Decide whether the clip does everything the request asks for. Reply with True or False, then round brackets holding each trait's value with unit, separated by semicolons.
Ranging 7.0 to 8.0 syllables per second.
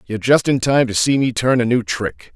False (5.4 syllables/s)